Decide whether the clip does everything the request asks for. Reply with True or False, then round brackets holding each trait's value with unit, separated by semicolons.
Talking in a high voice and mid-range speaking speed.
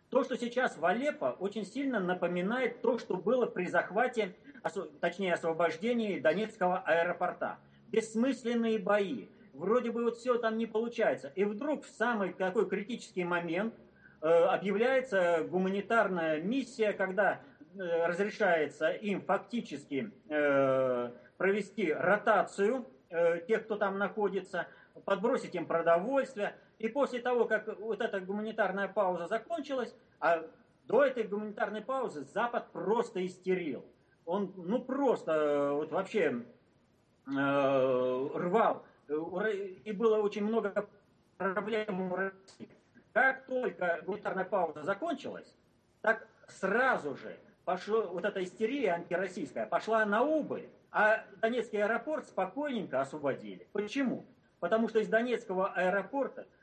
True (205 Hz; 120 wpm)